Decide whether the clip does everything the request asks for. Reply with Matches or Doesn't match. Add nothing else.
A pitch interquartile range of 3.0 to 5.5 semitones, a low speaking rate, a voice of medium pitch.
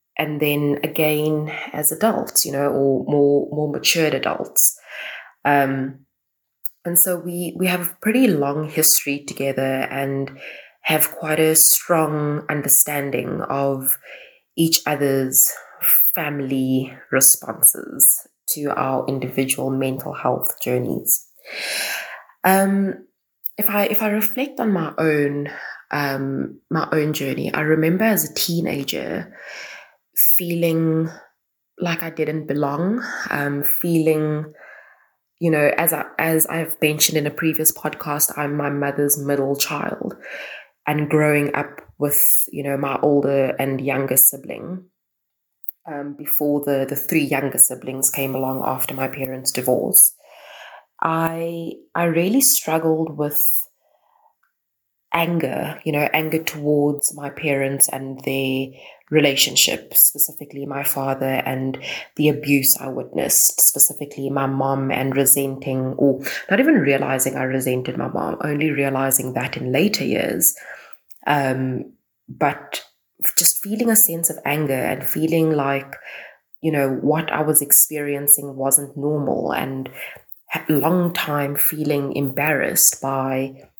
Doesn't match